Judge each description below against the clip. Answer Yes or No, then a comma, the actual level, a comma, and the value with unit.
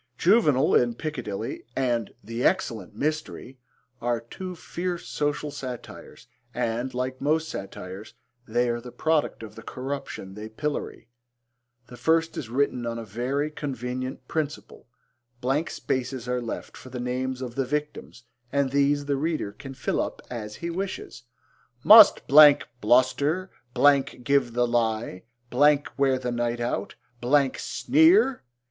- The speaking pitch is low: Yes, low, 130 Hz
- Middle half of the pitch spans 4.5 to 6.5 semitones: No, average, 3.8 semitones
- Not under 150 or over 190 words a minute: No, slow, 135 wpm